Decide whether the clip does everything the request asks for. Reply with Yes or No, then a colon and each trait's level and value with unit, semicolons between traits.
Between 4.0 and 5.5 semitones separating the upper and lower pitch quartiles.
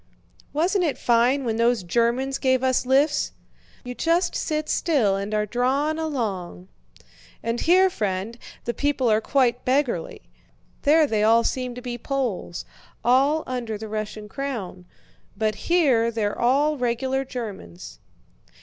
Yes: average, 4.3 semitones